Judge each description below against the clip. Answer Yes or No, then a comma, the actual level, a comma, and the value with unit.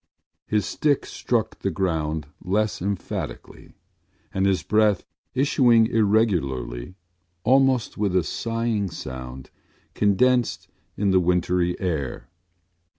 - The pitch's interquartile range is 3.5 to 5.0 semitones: Yes, average, 4.5 semitones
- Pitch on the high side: No, low, 100 Hz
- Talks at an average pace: No, slow, 100 wpm